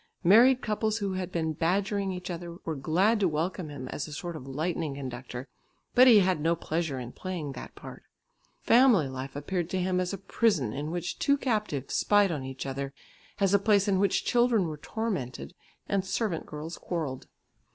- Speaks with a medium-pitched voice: Yes, medium, 175 Hz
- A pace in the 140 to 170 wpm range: No, average, 190 wpm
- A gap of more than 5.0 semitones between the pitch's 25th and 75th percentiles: Yes, wide, 5.4 semitones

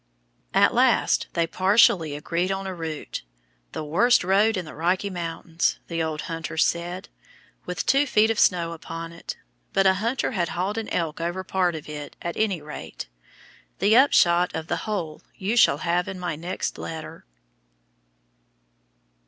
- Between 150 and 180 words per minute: Yes, average, 160 wpm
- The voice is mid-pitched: Yes, medium, 175 Hz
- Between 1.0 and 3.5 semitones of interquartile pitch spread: Yes, average, 2.9 semitones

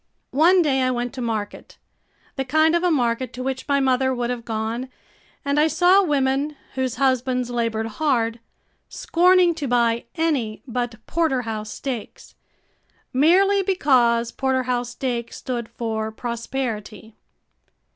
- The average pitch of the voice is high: Yes, very high, 255 Hz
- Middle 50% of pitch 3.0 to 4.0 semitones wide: Yes, average, 3.7 semitones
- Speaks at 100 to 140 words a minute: Yes, slow, 135 wpm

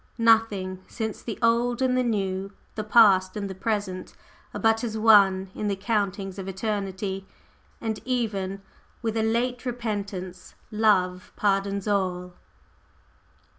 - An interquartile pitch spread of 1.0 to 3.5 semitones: Yes, average, 2.8 semitones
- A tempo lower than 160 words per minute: Yes, slow, 135 wpm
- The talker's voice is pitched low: No, high, 205 Hz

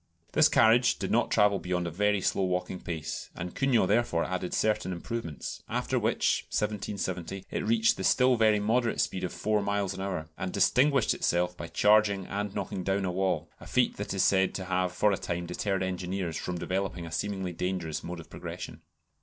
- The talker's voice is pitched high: No, very low, 95 Hz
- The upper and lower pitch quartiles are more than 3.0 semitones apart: No, narrow, 2.6 semitones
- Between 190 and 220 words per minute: Yes, average, 195 wpm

